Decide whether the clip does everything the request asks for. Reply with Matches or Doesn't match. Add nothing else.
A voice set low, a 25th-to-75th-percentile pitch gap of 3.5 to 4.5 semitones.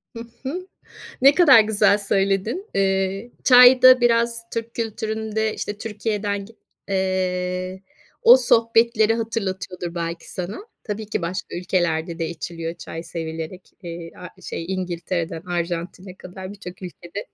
Doesn't match